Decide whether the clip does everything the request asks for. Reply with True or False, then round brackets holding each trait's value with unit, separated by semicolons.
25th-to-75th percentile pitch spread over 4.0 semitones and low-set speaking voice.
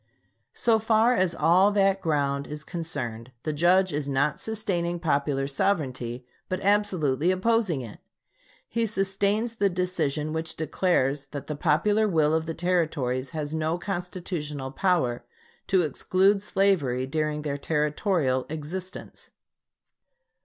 False (5.0 semitones; 165 Hz)